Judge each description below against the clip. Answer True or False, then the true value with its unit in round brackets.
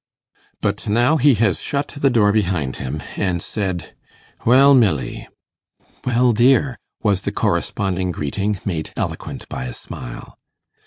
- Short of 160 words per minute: True (135 wpm)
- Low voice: True (105 Hz)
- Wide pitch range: True (5.8 semitones)